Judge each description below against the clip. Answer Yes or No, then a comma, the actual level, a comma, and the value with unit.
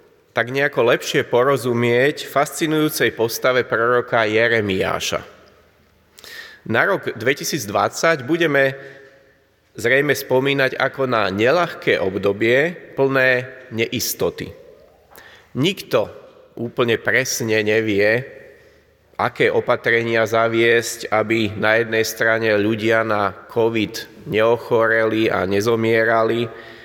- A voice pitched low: Yes, low, 115 Hz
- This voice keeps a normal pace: No, slow, 85 wpm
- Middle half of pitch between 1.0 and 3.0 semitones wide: No, average, 3.5 semitones